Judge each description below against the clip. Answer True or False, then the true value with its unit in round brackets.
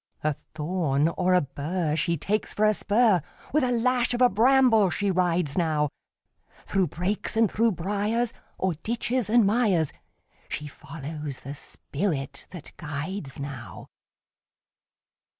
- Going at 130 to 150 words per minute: True (135 wpm)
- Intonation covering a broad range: True (6.4 semitones)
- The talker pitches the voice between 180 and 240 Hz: True (185 Hz)